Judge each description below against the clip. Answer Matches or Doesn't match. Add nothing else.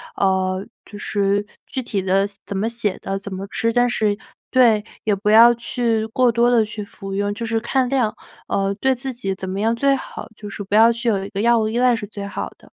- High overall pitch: Matches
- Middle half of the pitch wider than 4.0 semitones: Doesn't match